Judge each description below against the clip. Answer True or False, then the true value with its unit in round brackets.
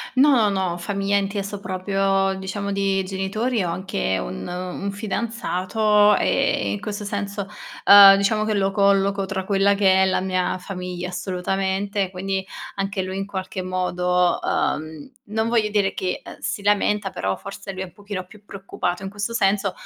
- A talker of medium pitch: False (195 Hz)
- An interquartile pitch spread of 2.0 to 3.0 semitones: False (1.6 semitones)